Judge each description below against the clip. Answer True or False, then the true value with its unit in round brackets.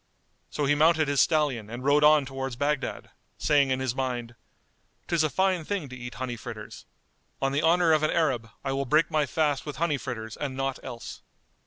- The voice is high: False (140 Hz)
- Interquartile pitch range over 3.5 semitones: False (3.2 semitones)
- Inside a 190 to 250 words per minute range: True (200 wpm)